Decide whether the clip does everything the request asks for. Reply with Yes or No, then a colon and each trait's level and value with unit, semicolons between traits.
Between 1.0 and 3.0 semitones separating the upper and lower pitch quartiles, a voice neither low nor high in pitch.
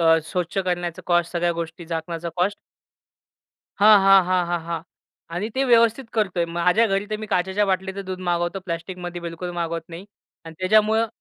Yes: narrow, 2.6 semitones; medium, 180 Hz